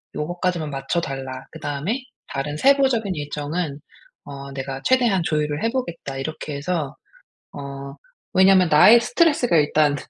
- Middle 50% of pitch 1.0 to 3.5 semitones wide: No, average, 5.2 semitones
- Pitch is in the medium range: Yes, medium, 150 Hz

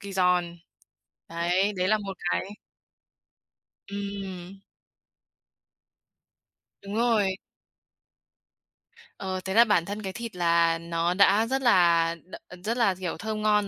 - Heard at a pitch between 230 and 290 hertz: No, high, 195 Hz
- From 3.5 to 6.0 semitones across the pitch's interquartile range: No, average, 3.0 semitones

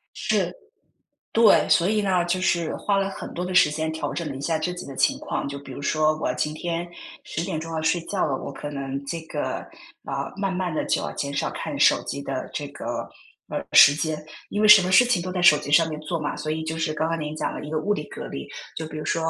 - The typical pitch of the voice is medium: Yes, medium, 160 Hz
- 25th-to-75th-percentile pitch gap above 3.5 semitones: No, average, 3.0 semitones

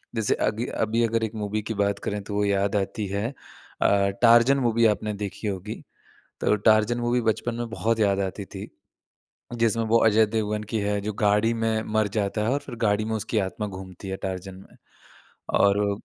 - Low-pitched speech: Yes, low, 105 Hz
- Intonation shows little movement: Yes, narrow, 1.9 semitones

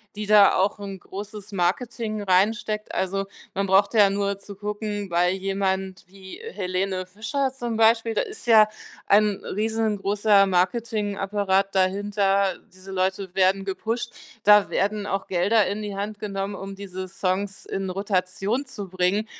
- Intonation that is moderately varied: No, narrow, 1.8 semitones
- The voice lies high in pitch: Yes, high, 200 Hz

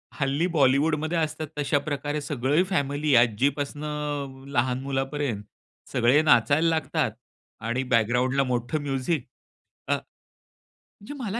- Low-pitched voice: No, medium, 145 Hz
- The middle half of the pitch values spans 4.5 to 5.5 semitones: No, average, 2.7 semitones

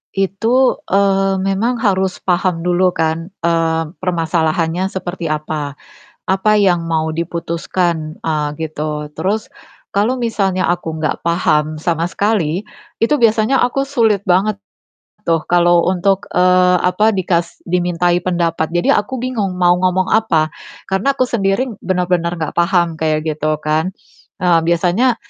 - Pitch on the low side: No, medium, 180 Hz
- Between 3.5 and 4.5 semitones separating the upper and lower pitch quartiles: No, average, 2.9 semitones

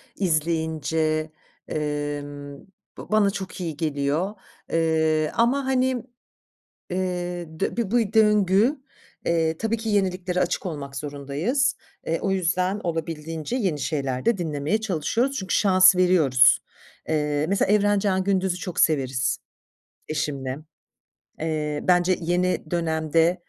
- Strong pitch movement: No, average, 4.2 semitones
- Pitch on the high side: No, medium, 170 Hz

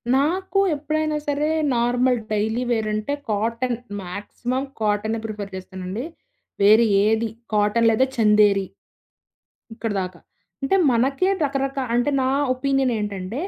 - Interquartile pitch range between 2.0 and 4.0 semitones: No, average, 4.4 semitones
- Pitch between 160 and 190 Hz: No, high, 230 Hz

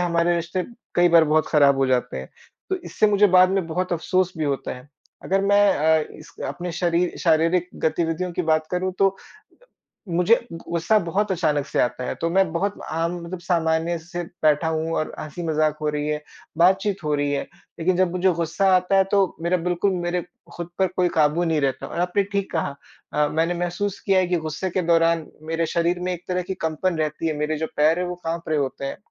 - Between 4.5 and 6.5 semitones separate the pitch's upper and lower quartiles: No, narrow, 2.5 semitones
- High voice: No, medium, 170 Hz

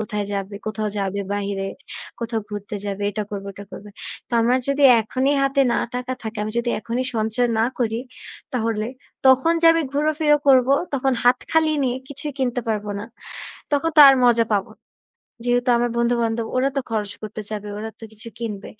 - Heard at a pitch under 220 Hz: No, high, 230 Hz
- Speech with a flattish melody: No, average, 3.6 semitones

